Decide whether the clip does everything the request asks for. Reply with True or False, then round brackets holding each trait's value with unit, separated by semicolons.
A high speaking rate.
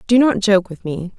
True (255 wpm)